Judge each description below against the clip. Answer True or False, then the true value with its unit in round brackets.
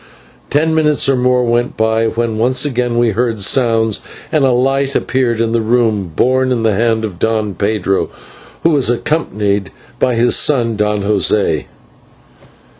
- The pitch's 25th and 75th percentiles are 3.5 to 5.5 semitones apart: False (2.7 semitones)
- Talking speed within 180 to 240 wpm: False (160 wpm)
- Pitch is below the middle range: True (115 Hz)